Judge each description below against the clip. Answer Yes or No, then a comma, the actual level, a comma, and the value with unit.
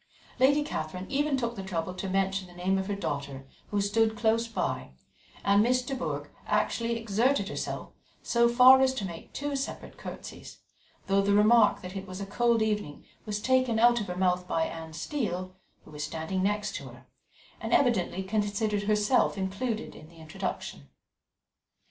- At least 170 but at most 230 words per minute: Yes, average, 175 wpm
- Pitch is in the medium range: No, high, 205 Hz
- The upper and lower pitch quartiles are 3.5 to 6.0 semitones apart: Yes, average, 4.3 semitones